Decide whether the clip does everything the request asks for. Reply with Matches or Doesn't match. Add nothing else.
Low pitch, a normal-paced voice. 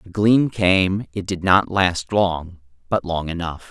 Matches